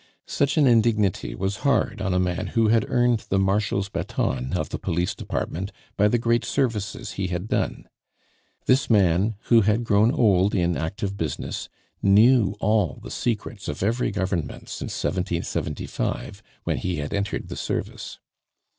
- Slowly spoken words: No, average, 155 wpm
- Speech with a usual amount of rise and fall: Yes, average, 3.8 semitones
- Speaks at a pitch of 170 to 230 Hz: No, low, 100 Hz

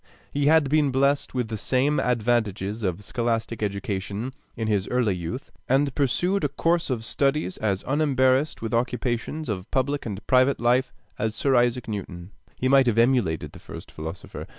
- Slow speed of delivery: No, average, 170 wpm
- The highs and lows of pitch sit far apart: No, average, 4.4 semitones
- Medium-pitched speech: No, low, 120 Hz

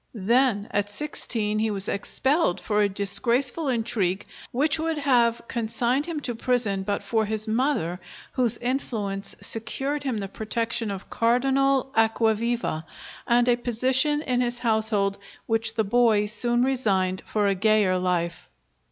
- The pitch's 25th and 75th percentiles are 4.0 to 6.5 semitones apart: No, average, 3.5 semitones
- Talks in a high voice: Yes, high, 230 Hz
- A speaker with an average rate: Yes, average, 145 wpm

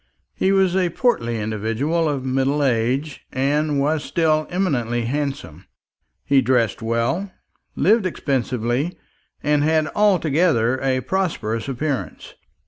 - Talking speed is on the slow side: Yes, slow, 115 wpm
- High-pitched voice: No, medium, 140 Hz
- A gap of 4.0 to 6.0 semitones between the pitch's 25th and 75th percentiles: Yes, average, 5.1 semitones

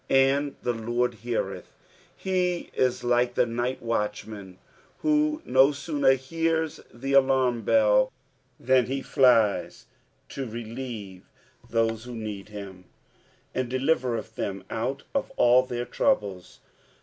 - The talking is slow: Yes, slow, 125 wpm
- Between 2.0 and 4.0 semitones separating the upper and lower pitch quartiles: Yes, average, 3.2 semitones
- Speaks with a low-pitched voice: Yes, low, 125 Hz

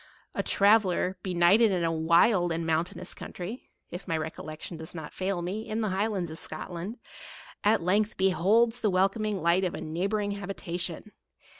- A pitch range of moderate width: Yes, average, 3.5 semitones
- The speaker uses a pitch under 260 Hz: Yes, medium, 185 Hz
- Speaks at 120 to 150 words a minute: No, average, 165 wpm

